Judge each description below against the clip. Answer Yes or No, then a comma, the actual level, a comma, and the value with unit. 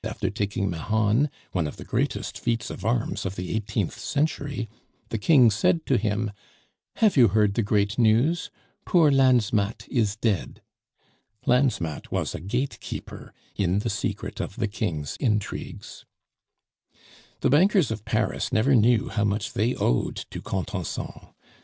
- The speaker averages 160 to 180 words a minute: No, average, 145 wpm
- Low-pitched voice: Yes, low, 110 Hz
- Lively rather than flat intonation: No, average, 3.7 semitones